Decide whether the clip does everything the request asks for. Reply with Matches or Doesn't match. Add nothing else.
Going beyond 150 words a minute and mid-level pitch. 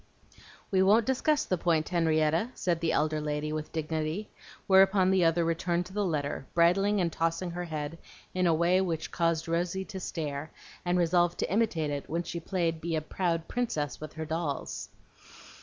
Matches